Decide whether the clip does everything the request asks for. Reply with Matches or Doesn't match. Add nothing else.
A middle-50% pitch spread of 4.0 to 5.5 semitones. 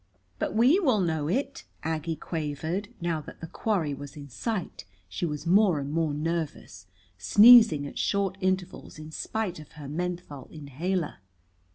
Matches